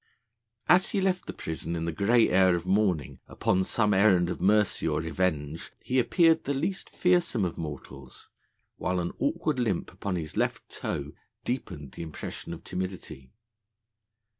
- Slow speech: No, average, 160 wpm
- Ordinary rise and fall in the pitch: No, wide, 6.5 semitones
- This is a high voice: No, very low, 95 Hz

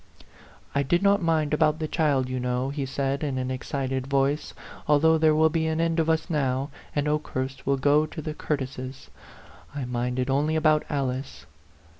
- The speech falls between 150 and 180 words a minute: No, average, 190 wpm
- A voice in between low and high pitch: Yes, medium, 145 Hz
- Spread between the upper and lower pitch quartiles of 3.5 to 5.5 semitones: No, average, 3.0 semitones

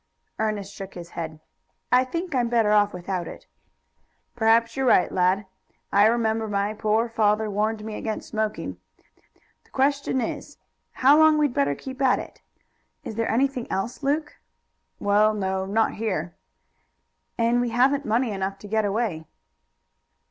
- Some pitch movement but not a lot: Yes, average, 3.3 semitones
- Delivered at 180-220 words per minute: No, average, 150 wpm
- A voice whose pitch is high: Yes, high, 220 Hz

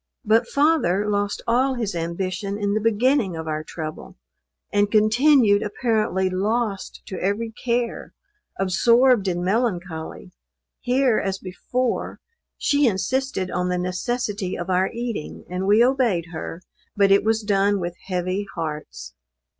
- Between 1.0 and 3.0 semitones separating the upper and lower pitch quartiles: No, average, 4.3 semitones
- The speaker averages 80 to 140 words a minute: Yes, slow, 135 wpm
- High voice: Yes, high, 205 Hz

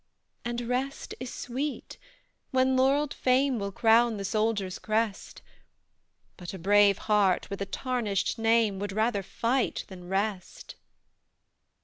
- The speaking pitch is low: No, high, 225 Hz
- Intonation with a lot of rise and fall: No, average, 4.0 semitones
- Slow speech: Yes, slow, 125 wpm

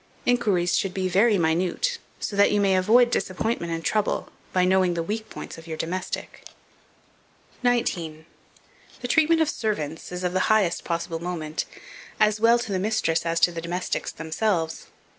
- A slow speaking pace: No, average, 165 wpm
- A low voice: No, medium, 185 Hz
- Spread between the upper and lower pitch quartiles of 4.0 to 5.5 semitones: Yes, average, 4.4 semitones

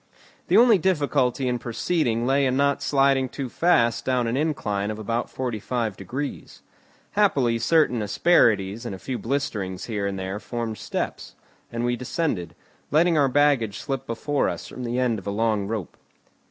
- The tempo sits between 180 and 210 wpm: No, average, 170 wpm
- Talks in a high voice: No, low, 120 Hz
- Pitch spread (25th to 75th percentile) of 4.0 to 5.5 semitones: Yes, average, 4.5 semitones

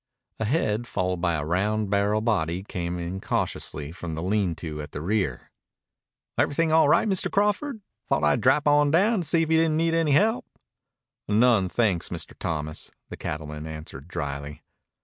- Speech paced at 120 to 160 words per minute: No, average, 175 wpm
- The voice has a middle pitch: No, low, 100 Hz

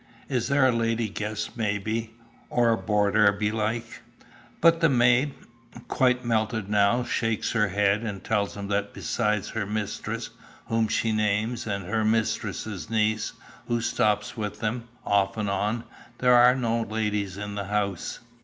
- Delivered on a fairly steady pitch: Yes, narrow, 2.2 semitones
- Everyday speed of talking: Yes, average, 155 wpm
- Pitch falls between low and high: No, low, 110 Hz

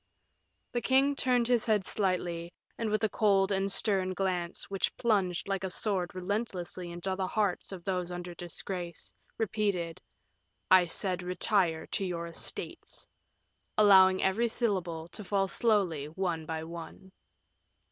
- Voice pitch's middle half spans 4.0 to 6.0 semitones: No, average, 2.9 semitones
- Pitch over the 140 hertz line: Yes, high, 190 Hz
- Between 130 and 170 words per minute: Yes, average, 140 wpm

